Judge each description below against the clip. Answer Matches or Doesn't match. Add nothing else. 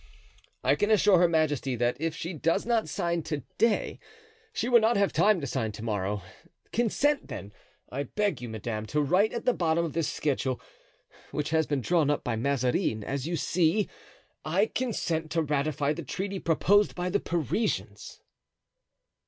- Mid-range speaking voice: Matches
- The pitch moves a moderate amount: Doesn't match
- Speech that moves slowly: Doesn't match